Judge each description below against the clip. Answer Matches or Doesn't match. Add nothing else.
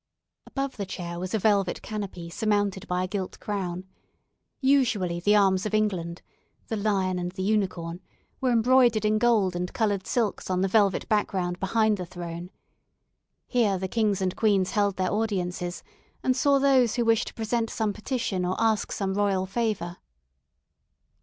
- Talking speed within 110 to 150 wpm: Doesn't match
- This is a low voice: Doesn't match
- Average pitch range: Matches